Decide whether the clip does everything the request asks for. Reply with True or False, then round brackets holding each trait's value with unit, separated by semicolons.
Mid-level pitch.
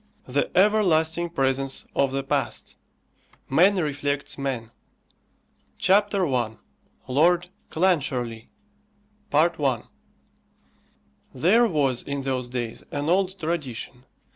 True (145 Hz)